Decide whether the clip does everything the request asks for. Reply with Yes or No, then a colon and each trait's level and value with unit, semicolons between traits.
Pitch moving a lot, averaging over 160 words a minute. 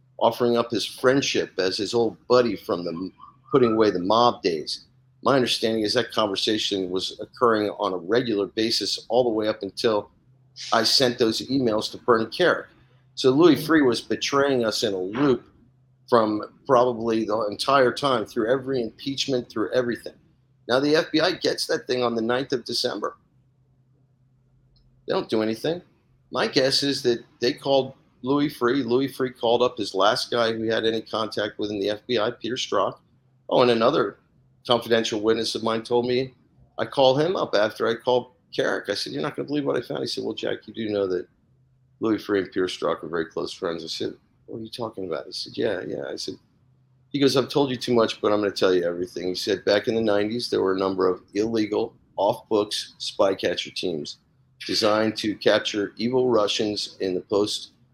No: average, 2.9 semitones; average, 200 wpm